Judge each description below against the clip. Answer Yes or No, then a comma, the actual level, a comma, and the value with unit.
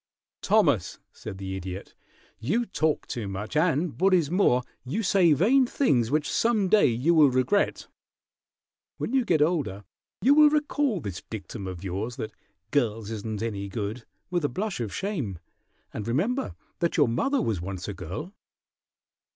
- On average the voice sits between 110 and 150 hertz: Yes, medium, 140 Hz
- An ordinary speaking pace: Yes, average, 160 wpm